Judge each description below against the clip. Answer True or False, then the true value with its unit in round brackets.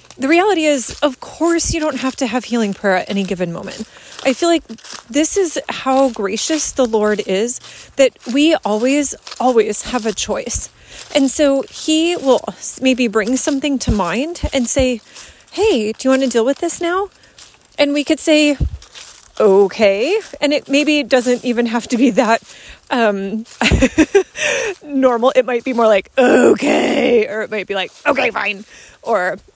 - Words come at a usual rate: True (170 wpm)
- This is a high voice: True (260 Hz)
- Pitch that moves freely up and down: False (4.6 semitones)